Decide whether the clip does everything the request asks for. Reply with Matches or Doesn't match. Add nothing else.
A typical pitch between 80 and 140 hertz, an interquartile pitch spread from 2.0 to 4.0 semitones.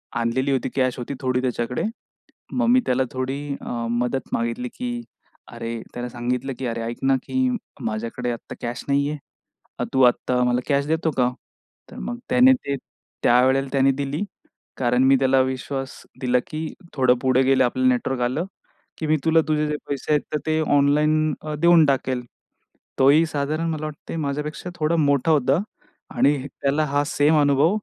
Matches